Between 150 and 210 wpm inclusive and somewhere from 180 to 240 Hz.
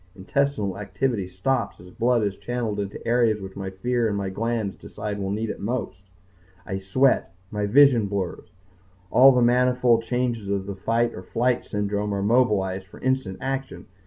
No: average, 175 wpm; low, 105 Hz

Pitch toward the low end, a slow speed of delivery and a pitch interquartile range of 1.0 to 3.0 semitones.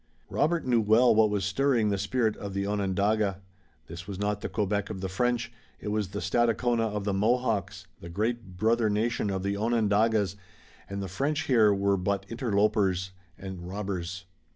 No: low, 105 Hz; average, 175 wpm; average, 2.7 semitones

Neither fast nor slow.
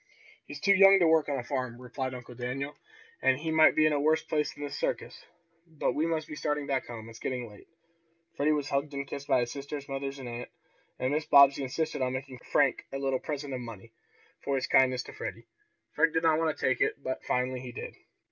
No: fast, 235 wpm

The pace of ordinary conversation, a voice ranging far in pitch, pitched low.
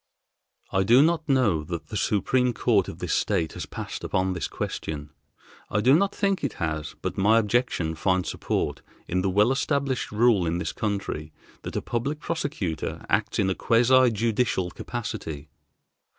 Yes: average, 165 wpm; wide, 6.0 semitones; low, 105 Hz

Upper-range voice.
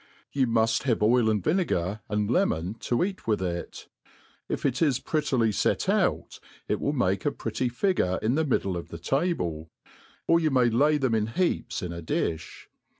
No: low, 115 Hz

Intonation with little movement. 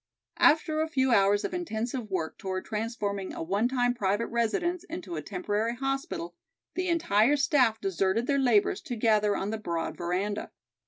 No: average, 5.2 semitones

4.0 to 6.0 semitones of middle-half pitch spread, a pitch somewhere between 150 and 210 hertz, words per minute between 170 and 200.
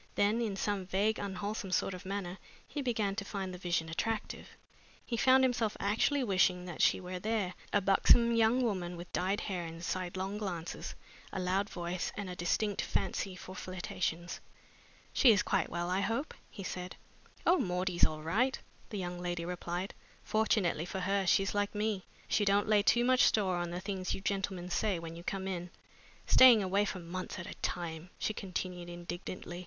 No: average, 2.7 semitones; high, 190 Hz; average, 185 wpm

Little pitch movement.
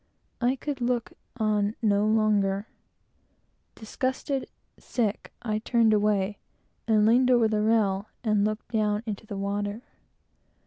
Yes: narrow, 2.1 semitones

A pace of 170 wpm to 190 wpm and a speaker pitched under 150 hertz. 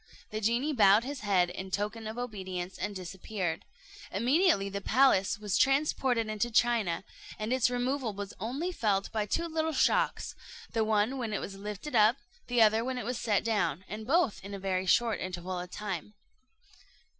No: average, 180 wpm; high, 215 Hz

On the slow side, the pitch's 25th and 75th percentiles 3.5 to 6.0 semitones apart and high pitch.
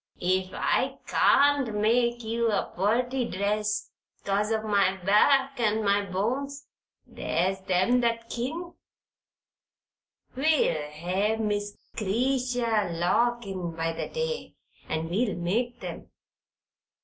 Yes: slow, 115 wpm; average, 4.4 semitones; high, 215 Hz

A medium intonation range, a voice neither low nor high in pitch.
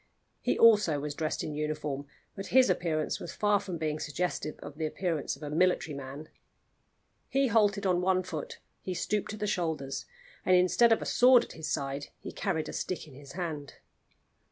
Yes: average, 5.0 semitones; medium, 165 Hz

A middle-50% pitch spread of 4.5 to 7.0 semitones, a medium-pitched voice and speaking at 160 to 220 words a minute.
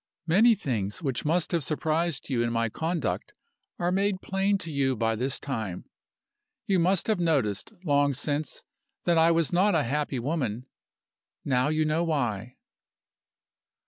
No: average, 5.3 semitones; medium, 150 Hz; average, 150 wpm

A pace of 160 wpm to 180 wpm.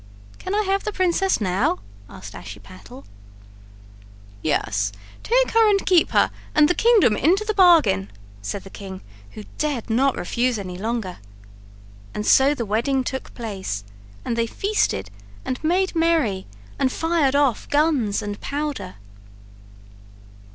No: slow, 135 wpm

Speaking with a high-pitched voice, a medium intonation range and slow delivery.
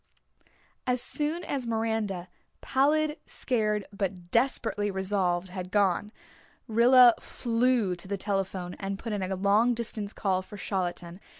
Yes: high, 205 Hz; average, 3.9 semitones; slow, 130 wpm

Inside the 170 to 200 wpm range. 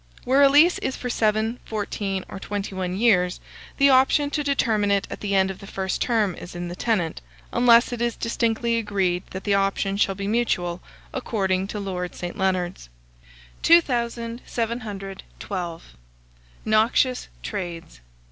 No: average, 150 wpm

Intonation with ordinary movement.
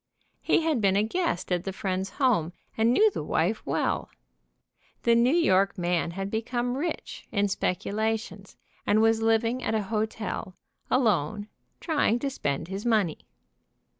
Yes: average, 3.8 semitones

